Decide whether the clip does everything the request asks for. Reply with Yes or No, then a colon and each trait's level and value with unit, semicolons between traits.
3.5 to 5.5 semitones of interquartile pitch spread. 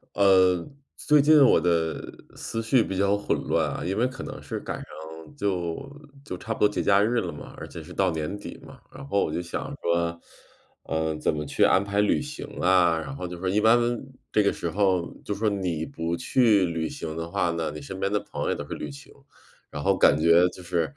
Yes: average, 3.9 semitones